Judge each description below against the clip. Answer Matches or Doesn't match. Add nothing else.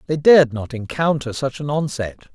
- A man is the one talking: Matches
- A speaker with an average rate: Matches